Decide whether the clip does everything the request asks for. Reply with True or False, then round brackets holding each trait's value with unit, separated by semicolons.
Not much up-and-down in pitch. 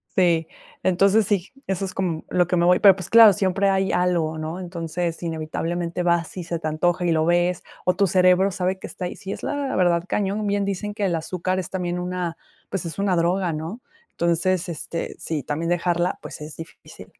True (2.2 semitones)